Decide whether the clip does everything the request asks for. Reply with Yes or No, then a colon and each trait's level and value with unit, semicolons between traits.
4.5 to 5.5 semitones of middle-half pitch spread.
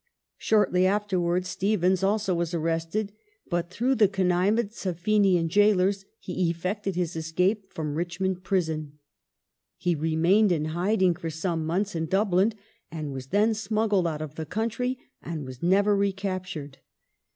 No: average, 3.6 semitones